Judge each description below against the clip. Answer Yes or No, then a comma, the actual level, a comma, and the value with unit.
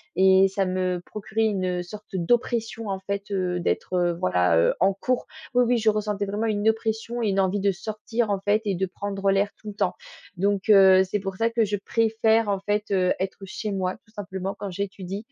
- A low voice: No, high, 200 Hz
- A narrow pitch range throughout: Yes, narrow, 2.2 semitones